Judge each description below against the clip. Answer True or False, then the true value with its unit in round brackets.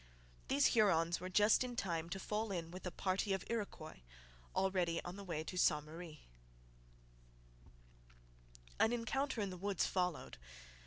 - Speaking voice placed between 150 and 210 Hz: True (185 Hz)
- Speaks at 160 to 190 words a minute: False (150 wpm)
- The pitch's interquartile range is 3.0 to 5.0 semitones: True (3.7 semitones)